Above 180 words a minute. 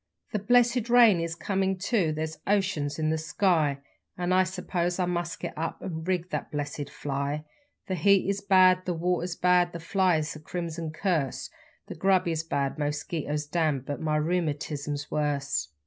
No: average, 165 wpm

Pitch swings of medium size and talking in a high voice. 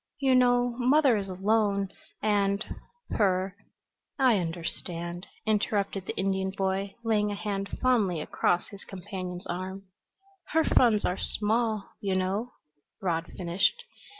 Yes: average, 3.1 semitones; high, 200 Hz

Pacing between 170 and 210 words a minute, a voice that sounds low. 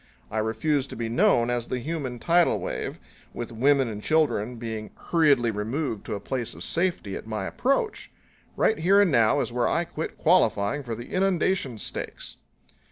Yes: average, 175 wpm; low, 125 Hz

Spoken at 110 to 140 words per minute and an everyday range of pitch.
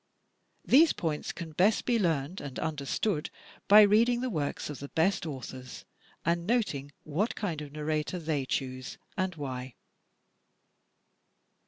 No: slow, 135 wpm; wide, 5.9 semitones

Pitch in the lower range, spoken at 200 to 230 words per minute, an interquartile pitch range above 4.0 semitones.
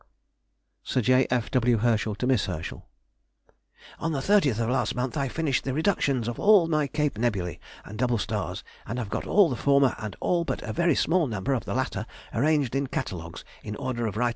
Yes: low, 125 Hz; fast, 205 wpm; average, 4.7 semitones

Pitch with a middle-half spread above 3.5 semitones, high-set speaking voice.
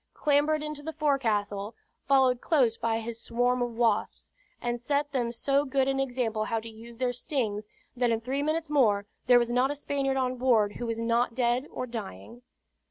No: average, 3.0 semitones; high, 245 Hz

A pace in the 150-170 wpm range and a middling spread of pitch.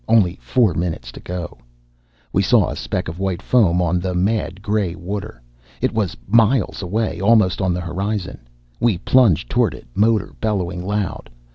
Yes: average, 165 wpm; average, 3.4 semitones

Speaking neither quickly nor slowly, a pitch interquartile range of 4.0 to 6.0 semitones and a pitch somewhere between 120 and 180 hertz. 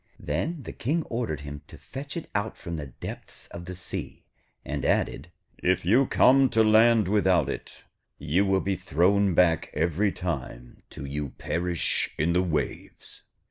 No: average, 165 wpm; wide, 5.5 semitones; very low, 90 Hz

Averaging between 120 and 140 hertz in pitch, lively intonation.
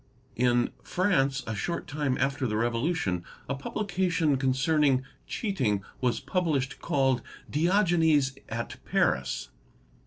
No: low, 135 Hz; average, 5.0 semitones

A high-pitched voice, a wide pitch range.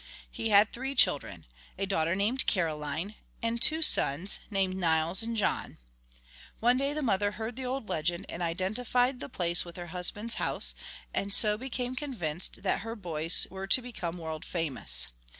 Yes: high, 195 Hz; wide, 5.8 semitones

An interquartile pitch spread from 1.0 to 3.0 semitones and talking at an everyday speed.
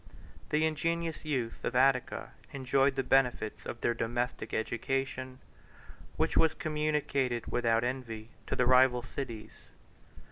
No: narrow, 2.6 semitones; slow, 130 wpm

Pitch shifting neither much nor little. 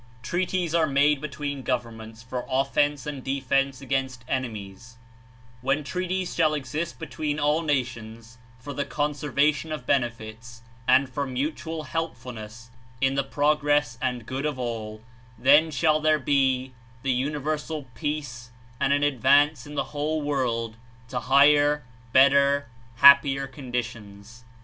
Yes: average, 3.0 semitones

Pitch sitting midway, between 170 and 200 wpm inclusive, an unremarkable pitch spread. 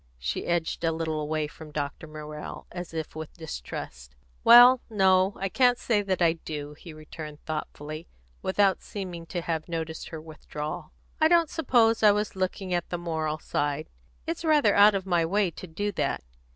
Yes: medium, 170 Hz; average, 180 wpm; average, 4.6 semitones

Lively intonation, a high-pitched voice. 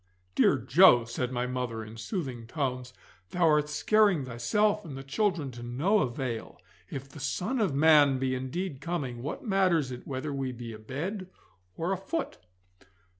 No: wide, 5.8 semitones; low, 135 Hz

